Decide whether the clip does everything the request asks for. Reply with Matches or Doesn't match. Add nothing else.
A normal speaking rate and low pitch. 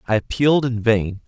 Matches